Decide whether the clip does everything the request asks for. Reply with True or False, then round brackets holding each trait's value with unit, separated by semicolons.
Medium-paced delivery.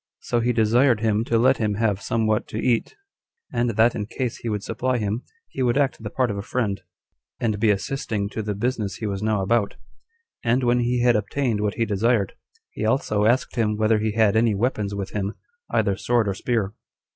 False (210 wpm)